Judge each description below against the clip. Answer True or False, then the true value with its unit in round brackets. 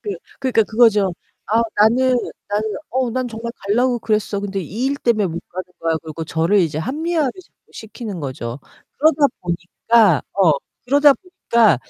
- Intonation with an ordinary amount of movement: False (6.1 semitones)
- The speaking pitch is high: True (220 Hz)